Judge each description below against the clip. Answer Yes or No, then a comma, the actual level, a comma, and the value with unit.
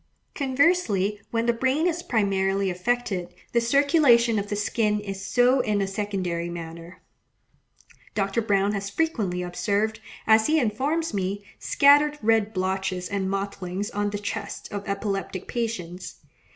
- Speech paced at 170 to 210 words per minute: No, average, 140 wpm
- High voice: Yes, high, 205 Hz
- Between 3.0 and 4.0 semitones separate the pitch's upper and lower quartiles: Yes, average, 3.6 semitones